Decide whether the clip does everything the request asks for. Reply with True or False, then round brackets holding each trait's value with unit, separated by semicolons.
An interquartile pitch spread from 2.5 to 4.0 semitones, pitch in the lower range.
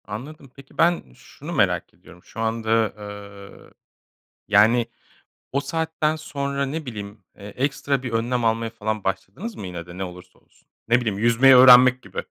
False (4.9 semitones; 115 Hz)